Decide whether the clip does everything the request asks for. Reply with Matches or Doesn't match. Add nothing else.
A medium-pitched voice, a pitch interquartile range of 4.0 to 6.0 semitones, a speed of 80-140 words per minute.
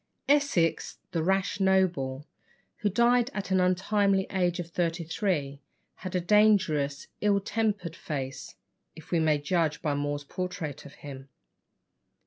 Matches